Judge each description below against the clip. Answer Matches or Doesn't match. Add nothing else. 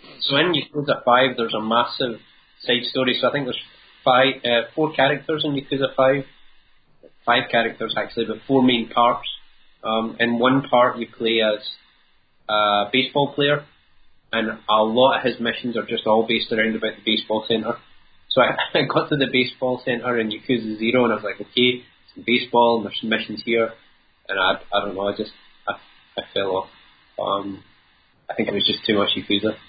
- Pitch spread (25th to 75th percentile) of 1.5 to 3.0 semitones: Matches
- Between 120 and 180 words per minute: Doesn't match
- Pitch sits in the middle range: Doesn't match